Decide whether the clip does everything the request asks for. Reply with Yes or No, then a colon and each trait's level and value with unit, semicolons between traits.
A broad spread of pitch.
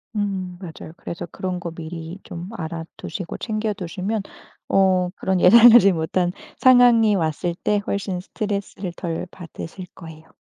No: average, 3.2 semitones